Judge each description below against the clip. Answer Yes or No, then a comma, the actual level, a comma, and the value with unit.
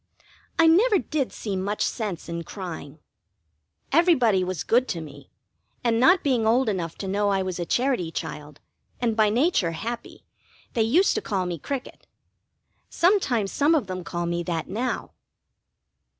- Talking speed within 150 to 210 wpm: Yes, average, 160 wpm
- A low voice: No, high, 210 Hz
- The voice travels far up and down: Yes, wide, 6.7 semitones